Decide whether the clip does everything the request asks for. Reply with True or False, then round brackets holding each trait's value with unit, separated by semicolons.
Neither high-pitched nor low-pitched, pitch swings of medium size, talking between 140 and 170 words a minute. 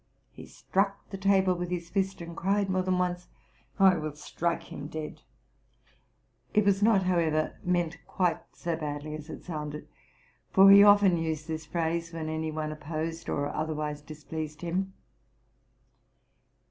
True (170 Hz; 3.2 semitones; 160 wpm)